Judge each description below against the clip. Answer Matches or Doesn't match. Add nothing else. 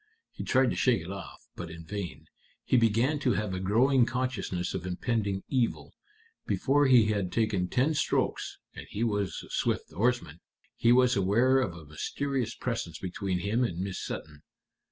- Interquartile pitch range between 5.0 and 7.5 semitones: Matches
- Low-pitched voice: Matches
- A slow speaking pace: Doesn't match